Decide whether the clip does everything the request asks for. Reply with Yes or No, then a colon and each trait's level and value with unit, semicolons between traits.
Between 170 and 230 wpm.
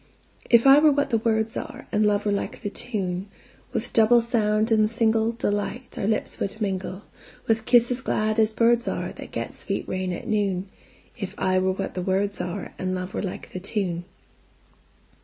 No: average, 160 wpm